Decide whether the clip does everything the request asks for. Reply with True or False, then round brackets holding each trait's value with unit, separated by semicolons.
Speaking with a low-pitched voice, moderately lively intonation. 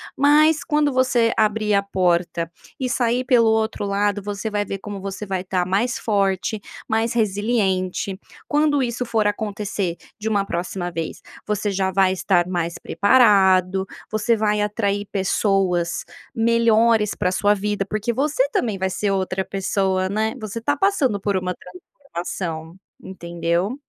False (205 Hz; 3.3 semitones)